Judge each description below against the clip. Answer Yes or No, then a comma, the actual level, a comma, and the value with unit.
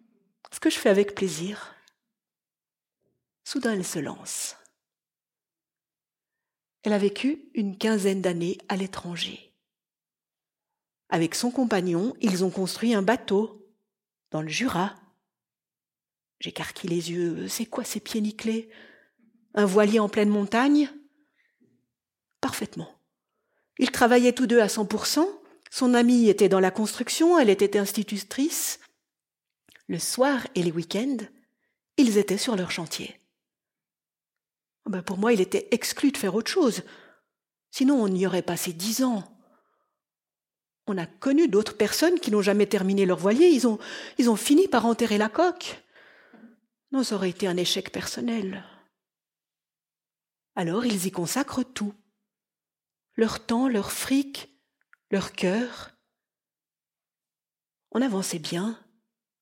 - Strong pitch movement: No, average, 4.2 semitones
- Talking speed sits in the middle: No, slow, 125 wpm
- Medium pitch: No, high, 215 Hz